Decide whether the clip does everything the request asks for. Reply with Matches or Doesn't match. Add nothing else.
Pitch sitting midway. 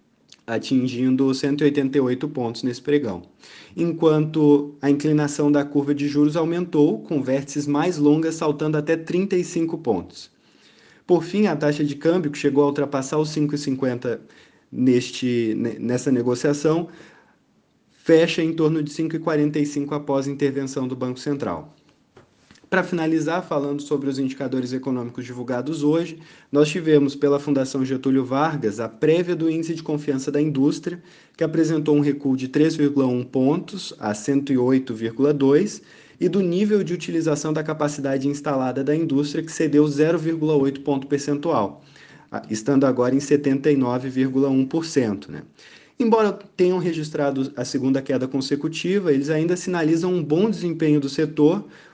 Matches